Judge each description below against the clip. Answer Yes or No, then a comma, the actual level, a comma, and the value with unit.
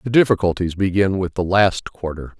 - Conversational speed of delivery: Yes, average, 175 wpm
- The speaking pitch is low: Yes, very low, 95 Hz